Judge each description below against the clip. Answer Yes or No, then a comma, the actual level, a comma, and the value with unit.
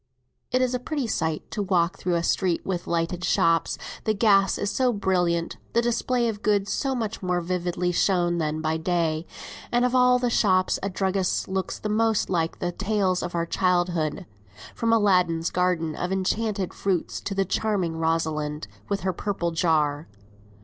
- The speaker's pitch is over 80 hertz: Yes, medium, 185 Hz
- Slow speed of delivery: No, average, 170 wpm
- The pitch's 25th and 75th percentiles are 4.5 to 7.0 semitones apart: No, average, 3.5 semitones